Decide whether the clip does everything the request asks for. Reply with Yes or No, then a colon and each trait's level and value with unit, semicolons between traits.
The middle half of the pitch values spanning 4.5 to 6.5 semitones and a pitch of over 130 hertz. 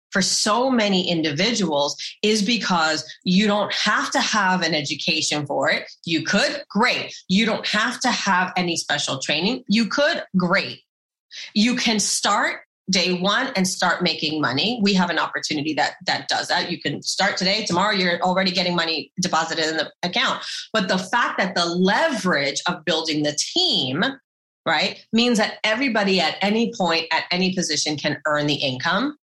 Yes: average, 4.8 semitones; medium, 185 Hz